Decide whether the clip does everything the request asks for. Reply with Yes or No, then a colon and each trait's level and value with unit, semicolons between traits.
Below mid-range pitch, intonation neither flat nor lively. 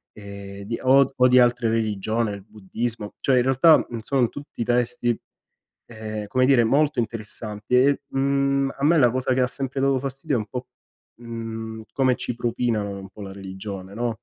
Yes: low, 120 Hz; average, 3.6 semitones